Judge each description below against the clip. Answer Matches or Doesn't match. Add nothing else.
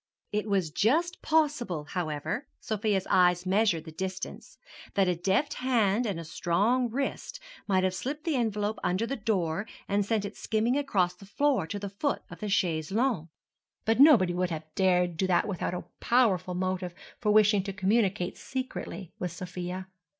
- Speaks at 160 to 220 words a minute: Matches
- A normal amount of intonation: Matches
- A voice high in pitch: Matches